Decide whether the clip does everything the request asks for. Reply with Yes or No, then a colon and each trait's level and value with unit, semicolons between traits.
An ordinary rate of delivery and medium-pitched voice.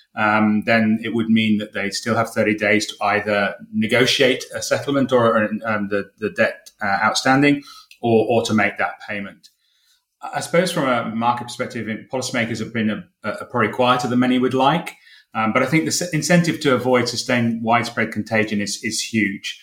No: average, 190 wpm; low, 115 Hz